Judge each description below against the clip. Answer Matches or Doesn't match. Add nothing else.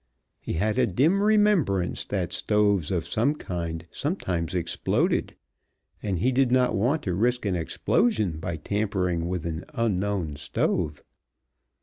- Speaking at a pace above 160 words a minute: Doesn't match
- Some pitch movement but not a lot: Doesn't match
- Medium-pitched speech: Doesn't match